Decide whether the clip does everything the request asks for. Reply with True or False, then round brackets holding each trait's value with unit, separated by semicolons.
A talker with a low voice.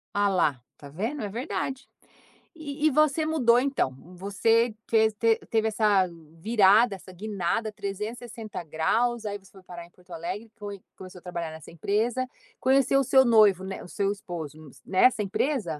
False (210 Hz)